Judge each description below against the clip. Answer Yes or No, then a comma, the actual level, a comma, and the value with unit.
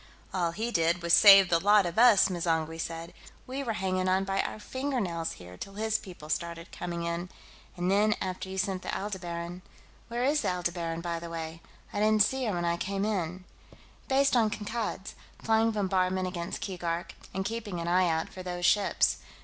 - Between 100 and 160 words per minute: No, average, 190 wpm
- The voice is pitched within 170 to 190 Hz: Yes, medium, 185 Hz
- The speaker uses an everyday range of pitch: Yes, average, 3.5 semitones